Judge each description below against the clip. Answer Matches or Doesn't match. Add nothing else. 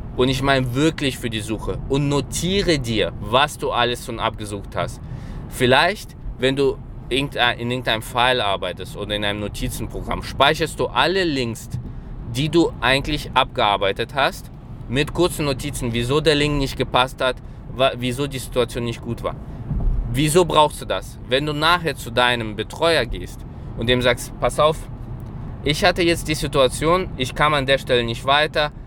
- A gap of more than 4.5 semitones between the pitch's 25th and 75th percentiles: Doesn't match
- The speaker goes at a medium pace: Matches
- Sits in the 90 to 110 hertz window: Doesn't match